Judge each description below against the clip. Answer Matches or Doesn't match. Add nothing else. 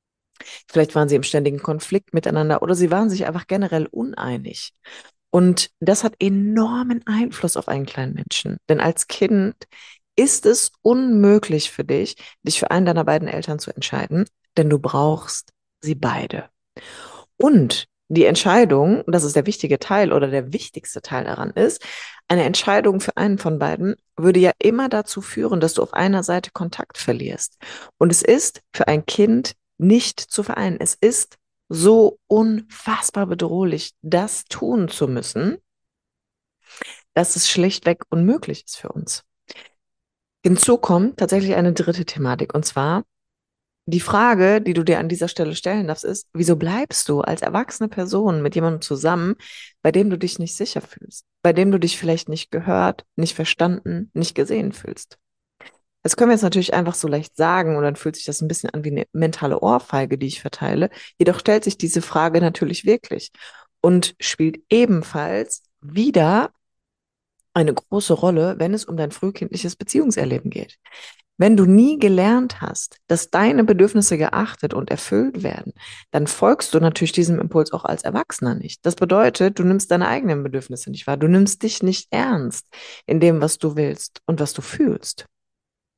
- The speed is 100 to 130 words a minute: Doesn't match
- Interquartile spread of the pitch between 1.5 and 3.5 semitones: Doesn't match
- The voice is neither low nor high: Matches